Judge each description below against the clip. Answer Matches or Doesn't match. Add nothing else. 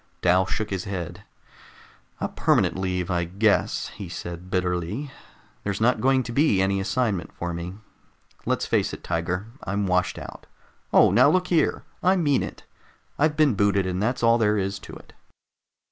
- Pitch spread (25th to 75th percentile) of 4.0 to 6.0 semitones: Matches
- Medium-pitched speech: Doesn't match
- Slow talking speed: Doesn't match